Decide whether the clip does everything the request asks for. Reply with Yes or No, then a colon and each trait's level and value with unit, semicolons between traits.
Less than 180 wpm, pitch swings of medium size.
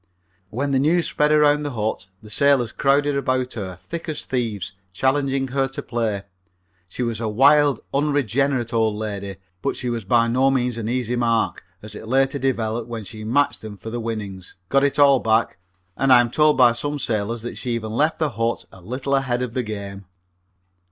No: average, 200 wpm; average, 3.8 semitones